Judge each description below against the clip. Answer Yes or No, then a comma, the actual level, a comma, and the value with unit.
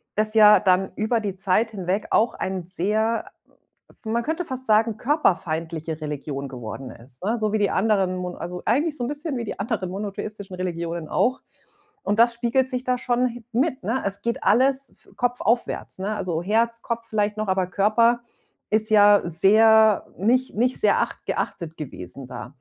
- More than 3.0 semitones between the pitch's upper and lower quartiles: Yes, average, 4.3 semitones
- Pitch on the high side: Yes, high, 215 Hz